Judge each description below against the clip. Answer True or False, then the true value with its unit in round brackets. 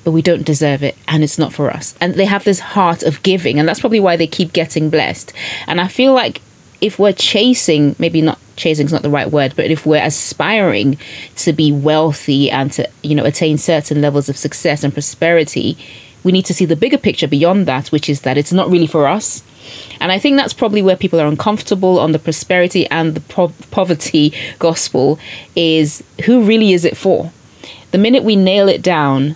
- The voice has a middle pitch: True (160 Hz)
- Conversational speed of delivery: False (215 wpm)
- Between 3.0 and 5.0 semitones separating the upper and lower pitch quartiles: True (4.0 semitones)